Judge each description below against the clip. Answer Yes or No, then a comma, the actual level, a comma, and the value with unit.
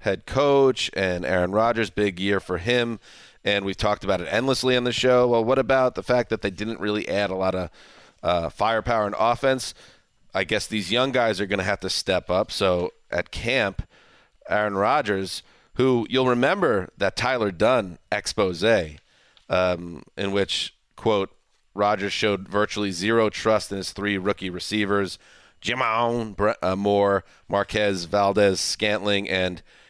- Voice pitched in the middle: No, low, 105 Hz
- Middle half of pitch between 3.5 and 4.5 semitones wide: No, average, 3.1 semitones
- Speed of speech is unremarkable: Yes, average, 160 wpm